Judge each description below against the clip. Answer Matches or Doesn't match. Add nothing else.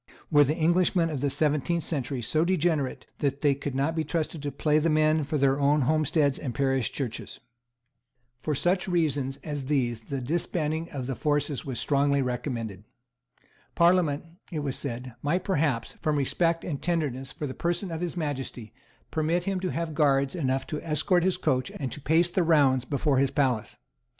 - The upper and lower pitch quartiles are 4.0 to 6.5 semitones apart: Doesn't match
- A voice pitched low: Doesn't match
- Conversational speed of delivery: Matches